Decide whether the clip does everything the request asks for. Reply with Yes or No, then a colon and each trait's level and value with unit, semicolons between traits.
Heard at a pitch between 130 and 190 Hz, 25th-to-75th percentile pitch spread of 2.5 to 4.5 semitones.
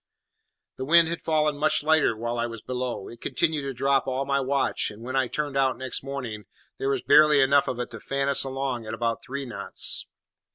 Yes: low, 135 Hz; average, 2.8 semitones